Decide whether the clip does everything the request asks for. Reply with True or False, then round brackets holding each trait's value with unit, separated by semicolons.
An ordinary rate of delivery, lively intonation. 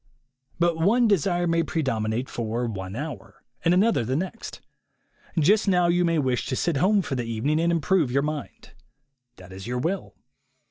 True (175 wpm; 6.3 semitones)